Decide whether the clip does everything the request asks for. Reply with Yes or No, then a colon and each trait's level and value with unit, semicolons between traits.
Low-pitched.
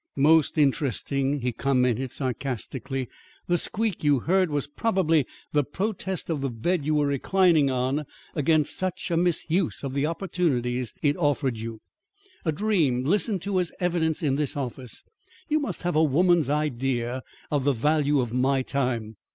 No: medium, 145 Hz